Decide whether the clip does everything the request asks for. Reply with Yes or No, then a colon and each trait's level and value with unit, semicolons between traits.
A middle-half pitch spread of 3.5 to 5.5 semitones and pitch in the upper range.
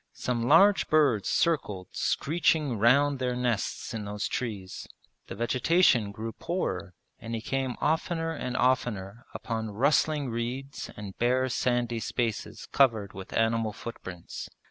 No: average, 4.0 semitones; low, 120 Hz